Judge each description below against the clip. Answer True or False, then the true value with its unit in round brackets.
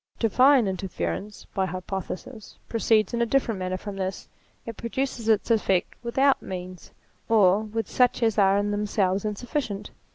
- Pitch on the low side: False (210 Hz)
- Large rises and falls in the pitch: False (3.3 semitones)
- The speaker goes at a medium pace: True (150 wpm)